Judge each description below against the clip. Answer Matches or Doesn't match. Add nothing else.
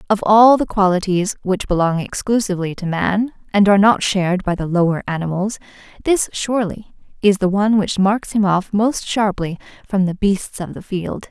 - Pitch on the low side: Doesn't match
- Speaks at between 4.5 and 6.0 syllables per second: Matches